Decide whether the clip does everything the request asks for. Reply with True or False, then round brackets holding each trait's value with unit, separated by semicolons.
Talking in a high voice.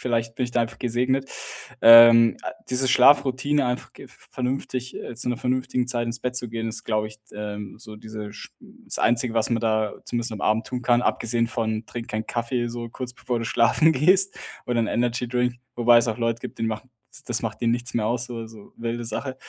False (120 Hz)